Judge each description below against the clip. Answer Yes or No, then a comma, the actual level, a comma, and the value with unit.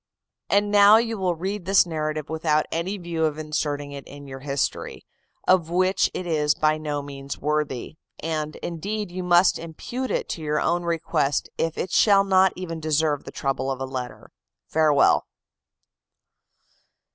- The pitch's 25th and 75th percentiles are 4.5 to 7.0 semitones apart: No, average, 3.8 semitones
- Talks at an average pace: Yes, average, 160 wpm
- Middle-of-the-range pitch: Yes, medium, 160 Hz